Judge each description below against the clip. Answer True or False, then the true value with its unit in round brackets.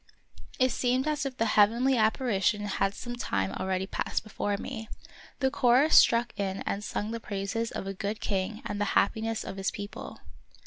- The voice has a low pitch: False (215 Hz)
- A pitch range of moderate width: True (3.5 semitones)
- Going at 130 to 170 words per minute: False (185 wpm)